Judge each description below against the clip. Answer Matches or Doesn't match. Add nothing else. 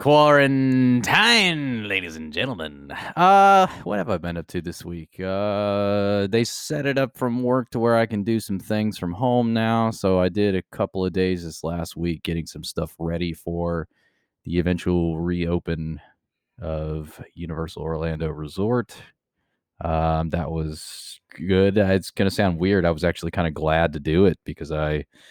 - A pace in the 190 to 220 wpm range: Doesn't match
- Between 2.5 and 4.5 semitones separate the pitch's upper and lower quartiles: Doesn't match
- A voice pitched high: Doesn't match